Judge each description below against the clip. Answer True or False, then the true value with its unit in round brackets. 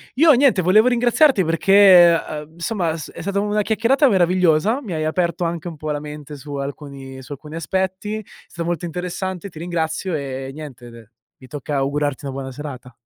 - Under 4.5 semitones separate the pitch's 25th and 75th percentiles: False (4.8 semitones)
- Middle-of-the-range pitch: True (165 Hz)